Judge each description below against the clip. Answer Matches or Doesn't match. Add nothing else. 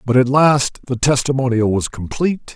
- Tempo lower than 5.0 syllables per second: Doesn't match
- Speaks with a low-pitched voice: Matches